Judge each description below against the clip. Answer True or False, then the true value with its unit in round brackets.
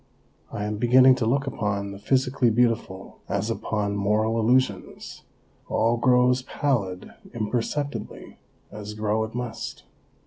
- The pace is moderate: False (125 wpm)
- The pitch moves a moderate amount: True (3.1 semitones)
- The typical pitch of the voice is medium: False (115 Hz)